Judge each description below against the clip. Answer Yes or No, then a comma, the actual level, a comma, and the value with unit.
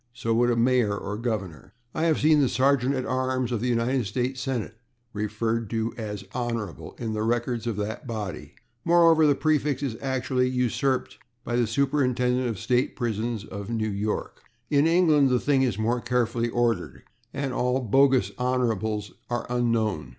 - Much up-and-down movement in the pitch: No, average, 2.8 semitones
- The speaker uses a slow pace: No, average, 165 wpm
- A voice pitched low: Yes, low, 120 Hz